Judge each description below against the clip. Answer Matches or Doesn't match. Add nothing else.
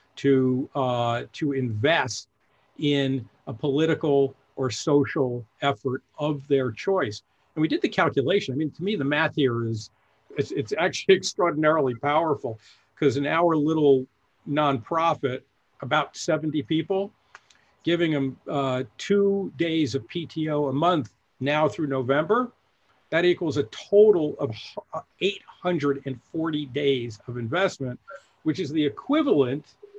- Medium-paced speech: Doesn't match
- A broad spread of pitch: Doesn't match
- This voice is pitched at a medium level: Matches